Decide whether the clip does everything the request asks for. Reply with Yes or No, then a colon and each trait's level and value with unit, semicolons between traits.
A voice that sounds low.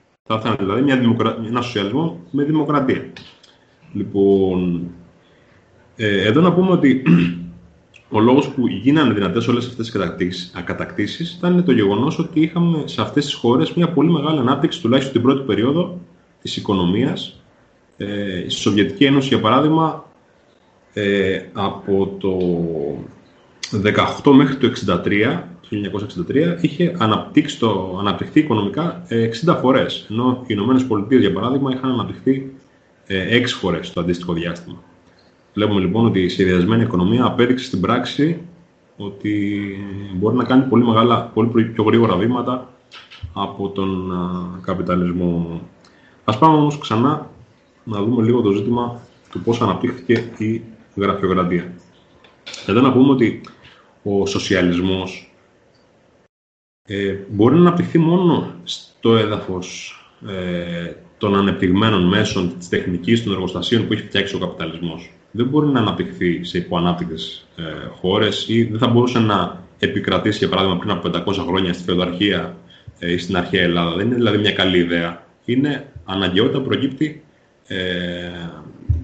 Yes: low, 105 Hz